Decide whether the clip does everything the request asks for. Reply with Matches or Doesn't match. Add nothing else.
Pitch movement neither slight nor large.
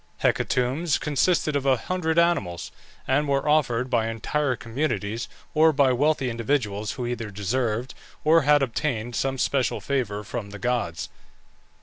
Matches